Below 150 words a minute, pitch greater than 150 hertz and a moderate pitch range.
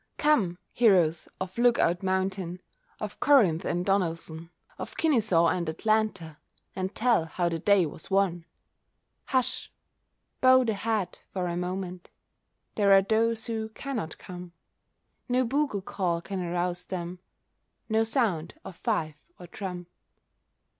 Yes: slow, 135 wpm; high, 190 Hz; average, 4.2 semitones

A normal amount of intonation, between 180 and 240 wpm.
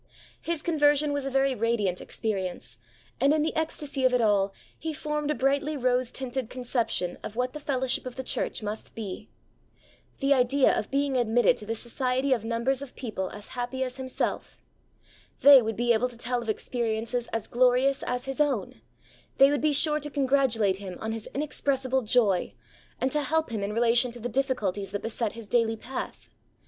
Yes: average, 3.4 semitones; average, 190 wpm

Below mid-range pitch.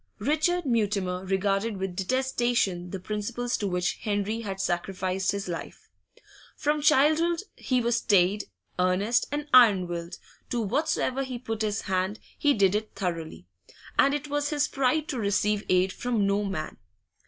No: high, 210 Hz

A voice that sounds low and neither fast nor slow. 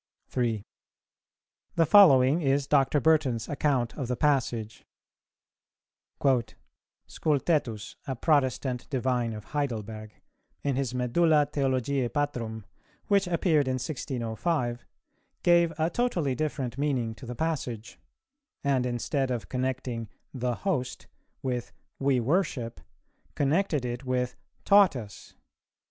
No: low, 130 Hz; slow, 110 wpm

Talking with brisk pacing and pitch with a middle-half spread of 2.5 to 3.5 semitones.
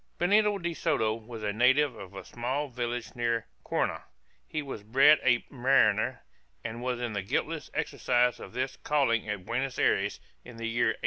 No: average, 180 wpm; average, 3.1 semitones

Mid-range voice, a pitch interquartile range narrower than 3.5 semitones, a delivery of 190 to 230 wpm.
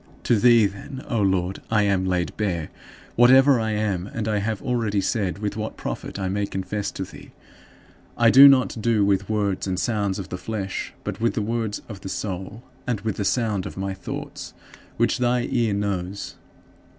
No: low, 105 Hz; average, 3.0 semitones; average, 195 wpm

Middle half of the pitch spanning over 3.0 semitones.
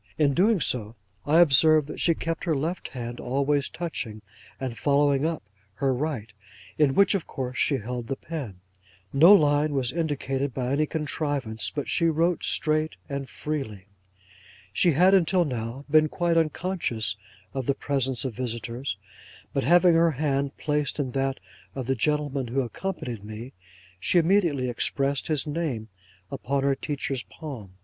Yes: average, 3.8 semitones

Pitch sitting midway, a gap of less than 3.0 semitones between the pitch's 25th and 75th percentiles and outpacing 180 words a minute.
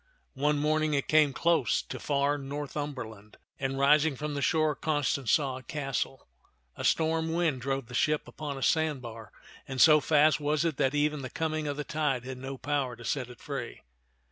Yes: medium, 145 Hz; narrow, 2.4 semitones; average, 195 wpm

